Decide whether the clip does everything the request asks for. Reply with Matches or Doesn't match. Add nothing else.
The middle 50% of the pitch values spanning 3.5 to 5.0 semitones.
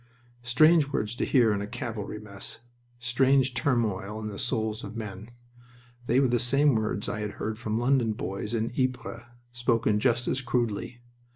Doesn't match